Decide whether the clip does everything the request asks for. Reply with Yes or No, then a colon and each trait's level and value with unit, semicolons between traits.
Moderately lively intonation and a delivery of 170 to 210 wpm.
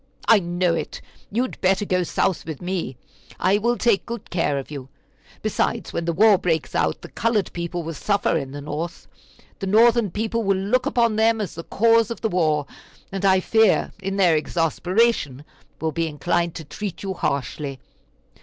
Yes: average, 4.9 semitones; average, 185 wpm